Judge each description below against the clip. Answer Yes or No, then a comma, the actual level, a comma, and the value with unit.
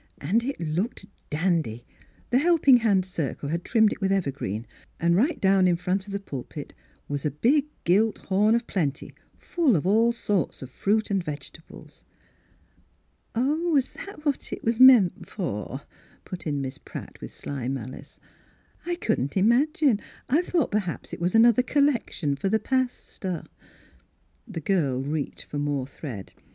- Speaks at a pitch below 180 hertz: No, high, 195 Hz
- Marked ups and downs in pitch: Yes, wide, 8.3 semitones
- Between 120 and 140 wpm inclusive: No, average, 165 wpm